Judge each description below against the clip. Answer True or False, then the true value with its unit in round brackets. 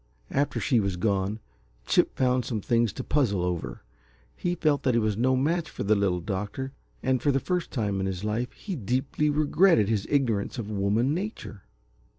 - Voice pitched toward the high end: False (120 Hz)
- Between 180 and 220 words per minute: True (185 wpm)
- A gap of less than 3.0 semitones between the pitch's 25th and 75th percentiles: False (5.6 semitones)